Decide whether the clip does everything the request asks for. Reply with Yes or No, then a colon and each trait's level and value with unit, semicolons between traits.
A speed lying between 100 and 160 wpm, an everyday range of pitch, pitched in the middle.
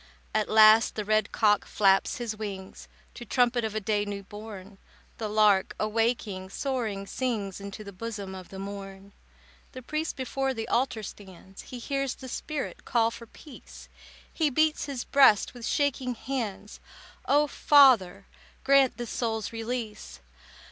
No: average, 150 wpm; average, 4.0 semitones; high, 220 Hz